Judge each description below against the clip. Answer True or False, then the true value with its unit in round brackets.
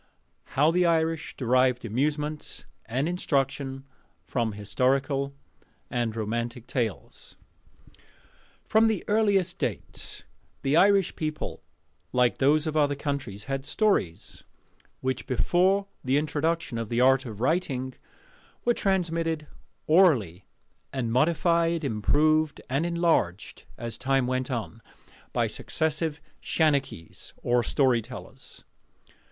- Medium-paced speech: False (105 wpm)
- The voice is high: False (140 Hz)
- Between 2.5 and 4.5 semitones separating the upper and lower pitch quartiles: False (4.9 semitones)